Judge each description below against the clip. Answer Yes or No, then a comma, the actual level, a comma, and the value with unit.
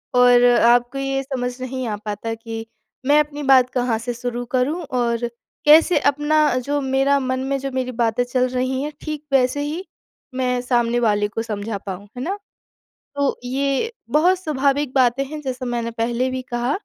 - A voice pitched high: Yes, very high, 255 Hz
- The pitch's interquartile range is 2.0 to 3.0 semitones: Yes, average, 2.7 semitones